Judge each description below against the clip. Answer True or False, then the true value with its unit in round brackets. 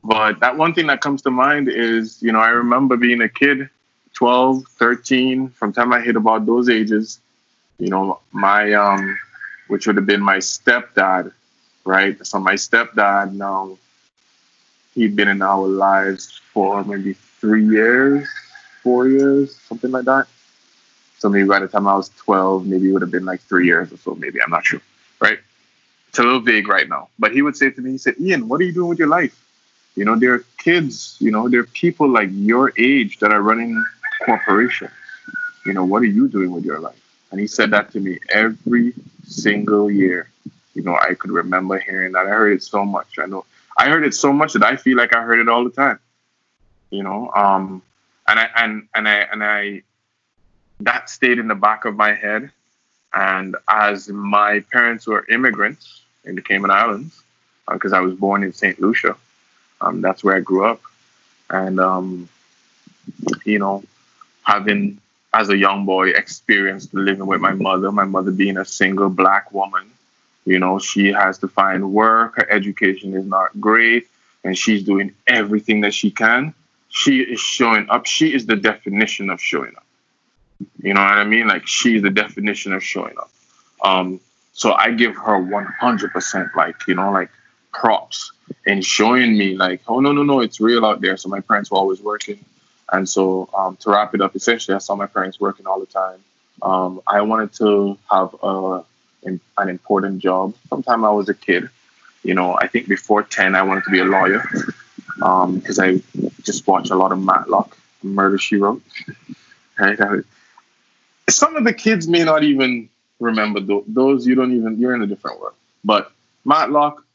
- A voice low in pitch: True (105 Hz)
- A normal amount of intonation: True (3.9 semitones)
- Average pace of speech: True (190 wpm)